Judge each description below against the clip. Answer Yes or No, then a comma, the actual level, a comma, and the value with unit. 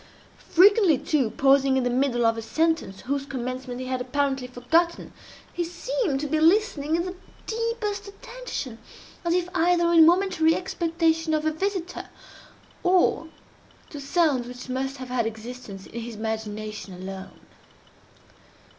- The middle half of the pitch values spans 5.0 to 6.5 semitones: Yes, wide, 5.6 semitones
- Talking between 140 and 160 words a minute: Yes, average, 145 wpm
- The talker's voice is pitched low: No, very high, 285 Hz